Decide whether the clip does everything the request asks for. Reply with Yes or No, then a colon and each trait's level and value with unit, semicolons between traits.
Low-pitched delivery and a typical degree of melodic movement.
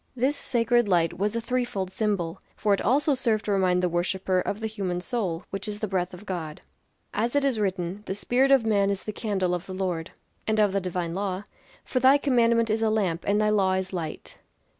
No: high, 200 Hz; average, 3.7 semitones